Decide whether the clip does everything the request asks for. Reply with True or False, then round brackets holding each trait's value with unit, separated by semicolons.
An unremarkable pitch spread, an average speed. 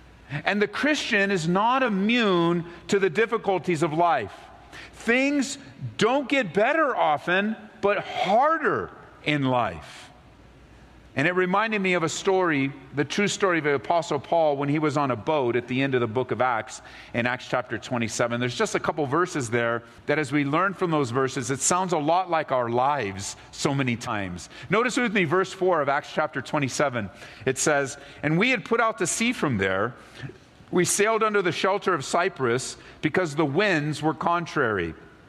False (6.9 semitones; 180 wpm)